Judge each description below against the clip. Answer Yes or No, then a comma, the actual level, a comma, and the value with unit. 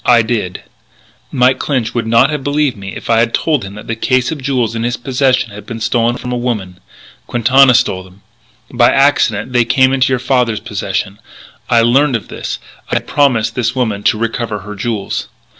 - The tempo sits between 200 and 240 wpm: Yes, fast, 205 wpm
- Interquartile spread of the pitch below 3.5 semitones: Yes, average, 2.8 semitones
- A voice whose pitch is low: Yes, low, 120 Hz